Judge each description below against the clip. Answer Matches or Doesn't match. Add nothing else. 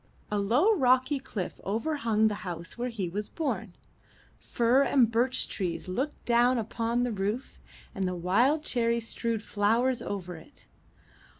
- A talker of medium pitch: Doesn't match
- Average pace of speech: Matches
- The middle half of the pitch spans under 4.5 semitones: Matches